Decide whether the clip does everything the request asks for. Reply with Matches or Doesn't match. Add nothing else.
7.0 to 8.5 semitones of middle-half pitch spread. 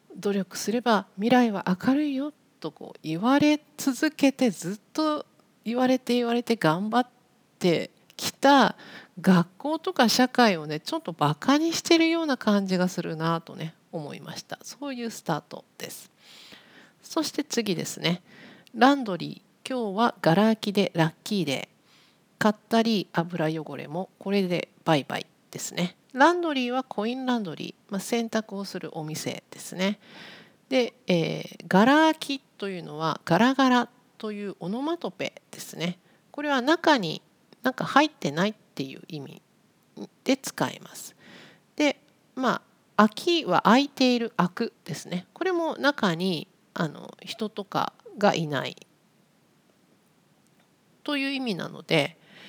Doesn't match